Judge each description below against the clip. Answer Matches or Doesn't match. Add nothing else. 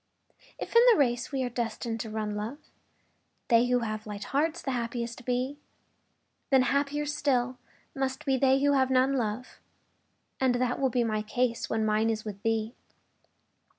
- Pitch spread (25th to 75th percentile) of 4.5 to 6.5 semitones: Doesn't match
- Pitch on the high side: Matches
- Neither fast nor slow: Matches